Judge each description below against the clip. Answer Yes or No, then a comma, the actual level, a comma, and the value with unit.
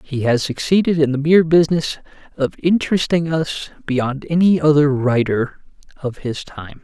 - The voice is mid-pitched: Yes, medium, 150 Hz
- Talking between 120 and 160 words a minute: Yes, average, 150 wpm